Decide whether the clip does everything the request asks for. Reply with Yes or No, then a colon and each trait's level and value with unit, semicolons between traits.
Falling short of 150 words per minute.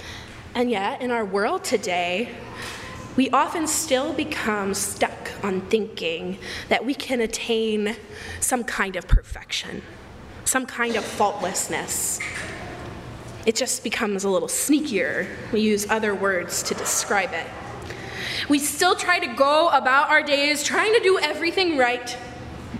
Yes: slow, 135 wpm